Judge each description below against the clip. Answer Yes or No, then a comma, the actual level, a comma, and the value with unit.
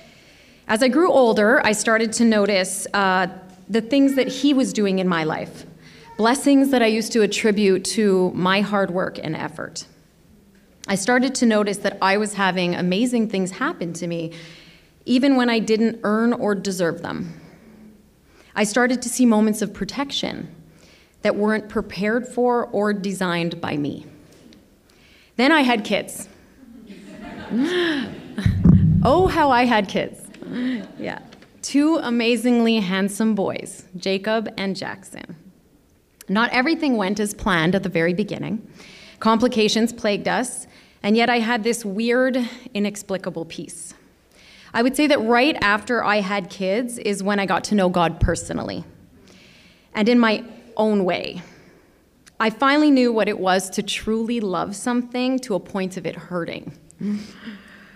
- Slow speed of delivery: No, average, 145 wpm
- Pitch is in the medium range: No, high, 215 Hz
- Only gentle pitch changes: No, average, 3.9 semitones